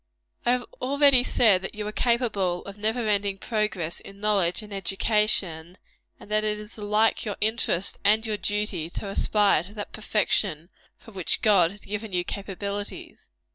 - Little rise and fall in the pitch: Yes, narrow, 1.8 semitones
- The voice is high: Yes, high, 210 Hz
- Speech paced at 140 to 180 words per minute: Yes, average, 170 wpm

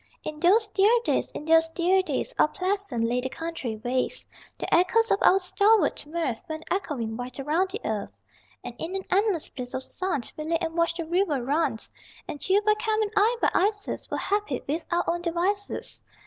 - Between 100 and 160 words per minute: No, average, 200 wpm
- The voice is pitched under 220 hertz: No, very high, 340 Hz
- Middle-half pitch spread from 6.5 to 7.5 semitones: No, average, 5.2 semitones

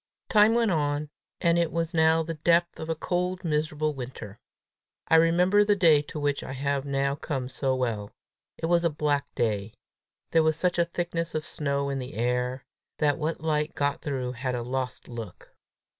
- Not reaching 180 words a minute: No, average, 190 wpm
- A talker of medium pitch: Yes, medium, 150 Hz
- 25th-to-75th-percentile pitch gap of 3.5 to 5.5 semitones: Yes, average, 4.0 semitones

